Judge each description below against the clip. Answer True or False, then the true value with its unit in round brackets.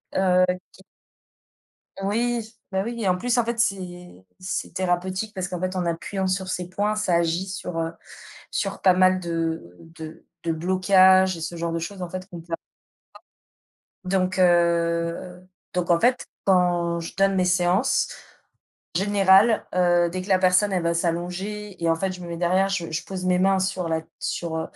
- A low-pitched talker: False (185 Hz)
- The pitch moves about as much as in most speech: False (1.9 semitones)